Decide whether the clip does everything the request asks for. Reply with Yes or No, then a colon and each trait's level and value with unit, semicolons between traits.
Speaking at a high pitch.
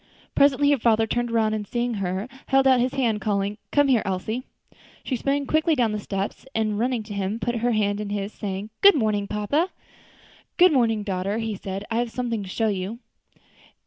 Yes: high, 220 Hz